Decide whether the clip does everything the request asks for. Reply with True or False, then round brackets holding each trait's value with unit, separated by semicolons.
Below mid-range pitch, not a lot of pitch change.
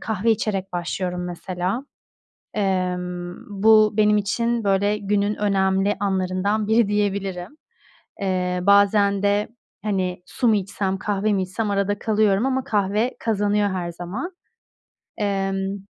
False (200 Hz; 1.9 semitones)